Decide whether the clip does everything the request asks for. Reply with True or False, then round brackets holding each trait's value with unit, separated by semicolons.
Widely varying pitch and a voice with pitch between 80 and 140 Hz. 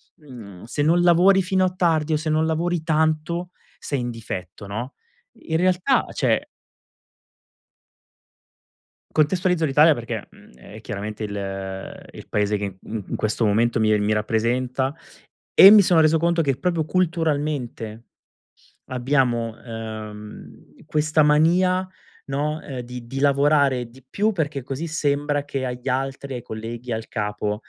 True (5.8 semitones; 135 Hz)